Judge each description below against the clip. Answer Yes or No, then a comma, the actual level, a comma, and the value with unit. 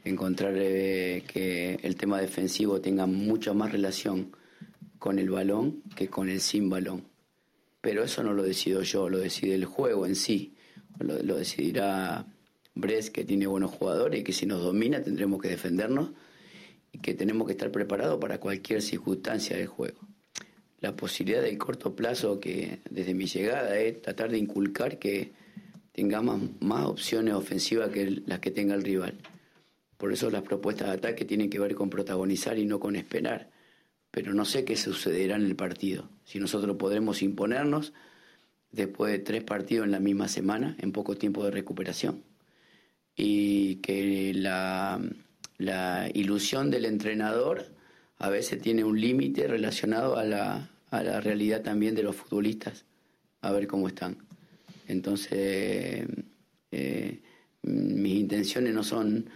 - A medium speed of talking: Yes, average, 155 wpm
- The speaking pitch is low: Yes, low, 100 Hz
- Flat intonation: Yes, narrow, 2.0 semitones